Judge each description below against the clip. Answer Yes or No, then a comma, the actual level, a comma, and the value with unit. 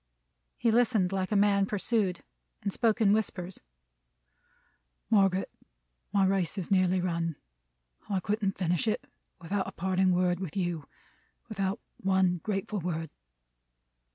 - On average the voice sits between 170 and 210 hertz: Yes, high, 190 Hz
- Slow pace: Yes, slow, 125 wpm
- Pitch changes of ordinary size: No, narrow, 2.2 semitones